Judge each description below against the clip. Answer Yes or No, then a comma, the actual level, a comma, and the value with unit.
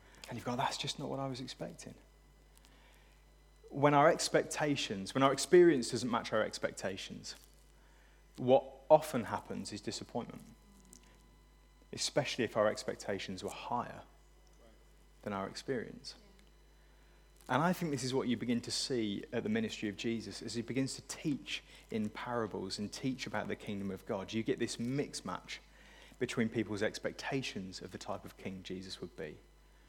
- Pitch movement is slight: No, average, 4.7 semitones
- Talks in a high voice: No, low, 120 Hz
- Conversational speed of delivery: Yes, average, 160 wpm